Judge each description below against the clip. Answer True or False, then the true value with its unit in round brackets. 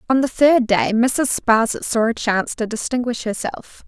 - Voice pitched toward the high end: True (235 Hz)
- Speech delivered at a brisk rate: False (185 wpm)